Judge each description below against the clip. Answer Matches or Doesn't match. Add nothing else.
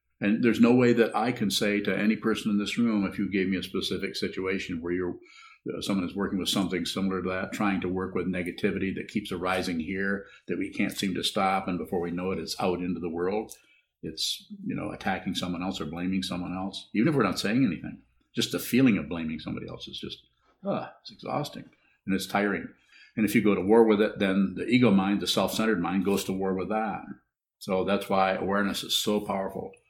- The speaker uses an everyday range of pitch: Doesn't match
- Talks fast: Matches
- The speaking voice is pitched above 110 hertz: Doesn't match